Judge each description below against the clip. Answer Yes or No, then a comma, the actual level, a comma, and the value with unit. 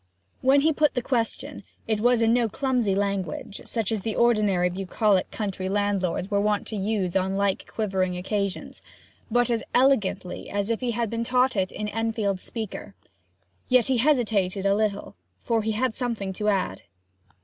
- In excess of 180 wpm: No, average, 170 wpm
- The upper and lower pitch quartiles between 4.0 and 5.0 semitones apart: No, average, 3.2 semitones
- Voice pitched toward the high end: Yes, high, 210 Hz